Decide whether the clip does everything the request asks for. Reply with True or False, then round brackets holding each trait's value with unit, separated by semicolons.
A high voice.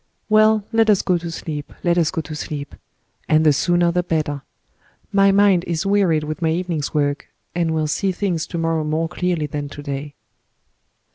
False (165 Hz)